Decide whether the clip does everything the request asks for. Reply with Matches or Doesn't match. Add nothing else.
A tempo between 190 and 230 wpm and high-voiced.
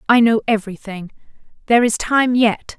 Doesn't match